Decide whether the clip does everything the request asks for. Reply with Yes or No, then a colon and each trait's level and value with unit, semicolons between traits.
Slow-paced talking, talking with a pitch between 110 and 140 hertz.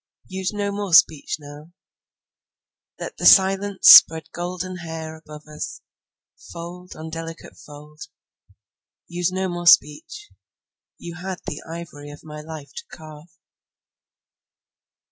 No: slow, 105 wpm; medium, 165 Hz